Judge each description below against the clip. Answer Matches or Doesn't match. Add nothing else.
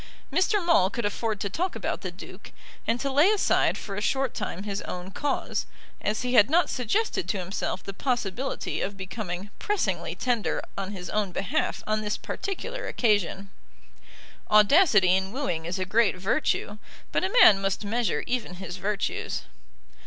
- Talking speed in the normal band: Matches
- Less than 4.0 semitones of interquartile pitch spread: Doesn't match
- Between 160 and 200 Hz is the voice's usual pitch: Doesn't match